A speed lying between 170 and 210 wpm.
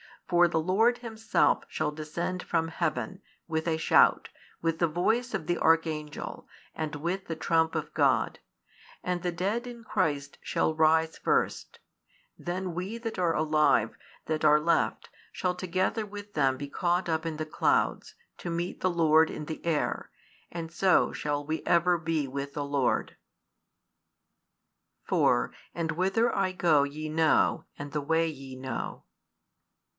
No: average, 155 wpm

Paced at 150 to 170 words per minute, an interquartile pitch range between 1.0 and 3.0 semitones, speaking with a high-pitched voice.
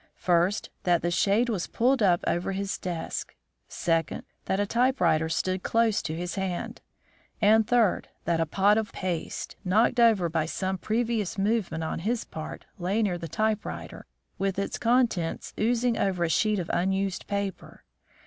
No: average, 160 wpm; average, 4.1 semitones; high, 195 Hz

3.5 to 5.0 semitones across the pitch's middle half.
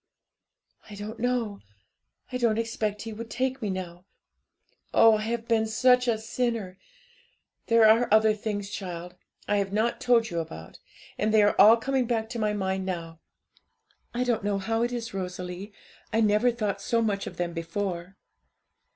No: average, 2.9 semitones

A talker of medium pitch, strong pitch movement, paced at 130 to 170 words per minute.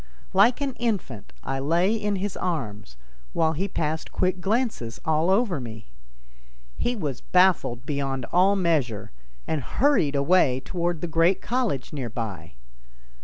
Yes: medium, 165 Hz; wide, 6.5 semitones; average, 140 wpm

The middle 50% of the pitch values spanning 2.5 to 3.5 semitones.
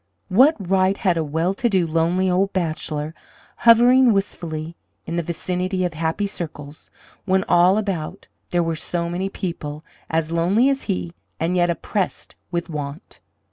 Yes: average, 3.0 semitones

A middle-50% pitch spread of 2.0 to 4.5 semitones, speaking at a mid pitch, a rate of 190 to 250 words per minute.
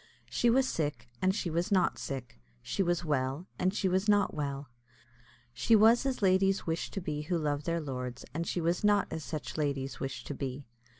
No: average, 5.2 semitones; medium, 165 Hz; average, 200 wpm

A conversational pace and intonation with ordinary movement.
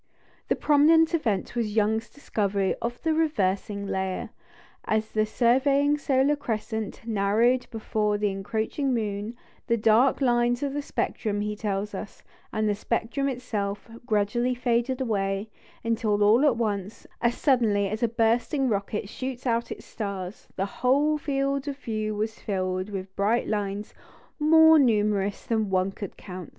Yes: average, 150 wpm; average, 3.8 semitones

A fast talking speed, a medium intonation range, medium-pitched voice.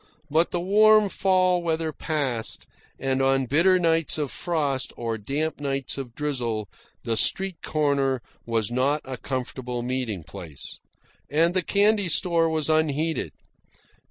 No: slow, 135 wpm; average, 4.6 semitones; medium, 145 Hz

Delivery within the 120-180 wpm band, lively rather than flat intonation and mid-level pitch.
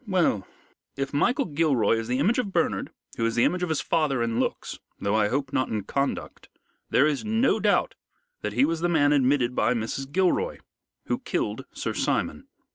No: average, 195 wpm; wide, 6.5 semitones; medium, 145 Hz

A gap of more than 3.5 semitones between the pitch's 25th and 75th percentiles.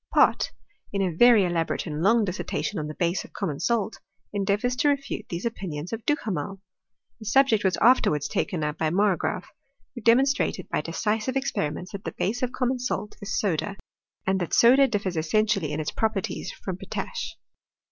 Yes: average, 5.2 semitones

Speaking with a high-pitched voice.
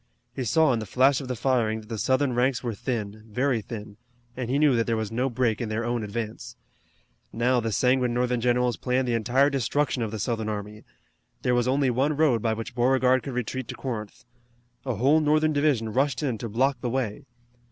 No: low, 125 Hz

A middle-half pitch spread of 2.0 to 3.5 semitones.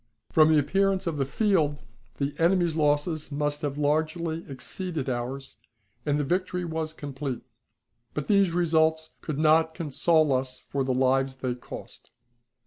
Yes: average, 3.1 semitones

